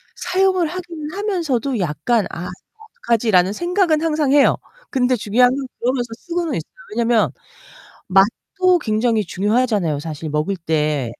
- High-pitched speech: Yes, high, 245 Hz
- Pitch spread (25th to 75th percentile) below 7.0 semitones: No, wide, 8.9 semitones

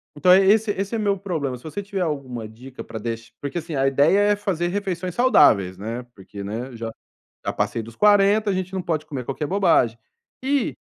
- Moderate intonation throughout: No, wide, 8.2 semitones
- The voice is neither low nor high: Yes, medium, 165 Hz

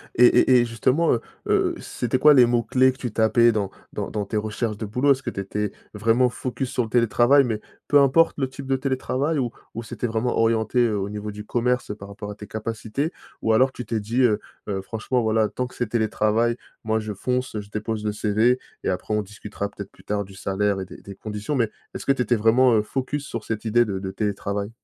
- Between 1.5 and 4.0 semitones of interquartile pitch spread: Yes, average, 3.1 semitones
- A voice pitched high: No, low, 115 Hz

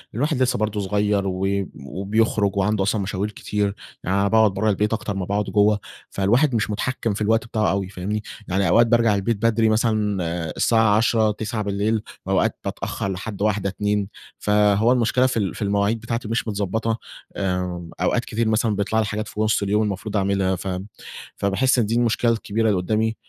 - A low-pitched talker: Yes, low, 105 Hz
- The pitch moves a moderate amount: No, narrow, 2.1 semitones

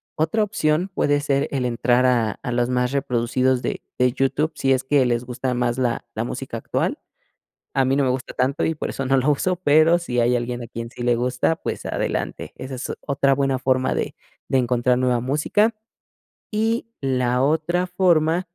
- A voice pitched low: Yes, low, 130 Hz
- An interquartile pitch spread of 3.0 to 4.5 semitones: Yes, average, 3.6 semitones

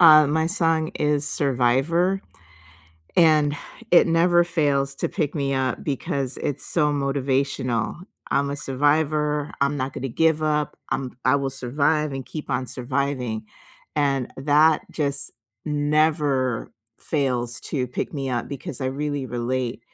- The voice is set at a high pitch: No, medium, 140 Hz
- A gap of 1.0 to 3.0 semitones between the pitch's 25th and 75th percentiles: Yes, narrow, 2.6 semitones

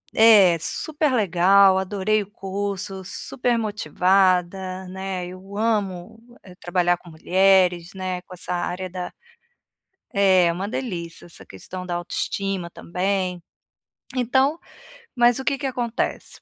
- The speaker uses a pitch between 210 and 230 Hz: No, high, 190 Hz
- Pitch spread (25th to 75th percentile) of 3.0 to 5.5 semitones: No, narrow, 2.5 semitones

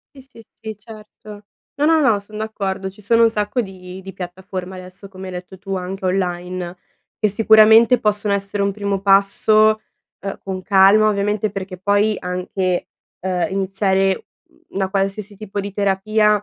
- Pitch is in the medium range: No, high, 200 Hz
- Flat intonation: Yes, narrow, 2.0 semitones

